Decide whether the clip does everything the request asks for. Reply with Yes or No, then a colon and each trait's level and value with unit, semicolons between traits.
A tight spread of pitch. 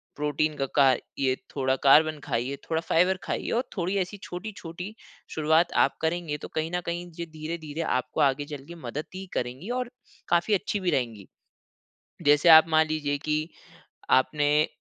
No: average, 3.1 semitones